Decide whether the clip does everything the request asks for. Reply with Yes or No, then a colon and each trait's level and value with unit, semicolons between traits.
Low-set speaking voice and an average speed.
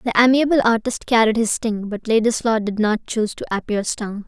No: high, 225 Hz; average, 195 wpm